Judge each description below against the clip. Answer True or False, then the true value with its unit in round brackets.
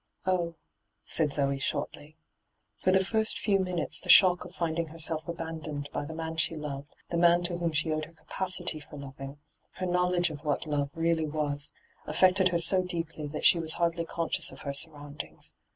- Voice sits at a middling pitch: True (165 Hz)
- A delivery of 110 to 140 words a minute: False (200 wpm)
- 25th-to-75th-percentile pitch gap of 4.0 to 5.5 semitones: False (2.7 semitones)